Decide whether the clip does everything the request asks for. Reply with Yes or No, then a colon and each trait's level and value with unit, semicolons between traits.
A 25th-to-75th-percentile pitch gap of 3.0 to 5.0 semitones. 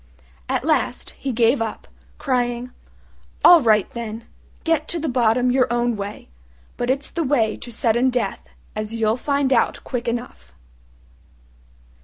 No: narrow, 2.6 semitones